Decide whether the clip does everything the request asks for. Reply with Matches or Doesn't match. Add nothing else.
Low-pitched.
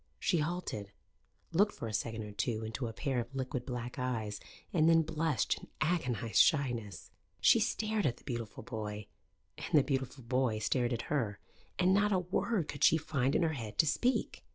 Matches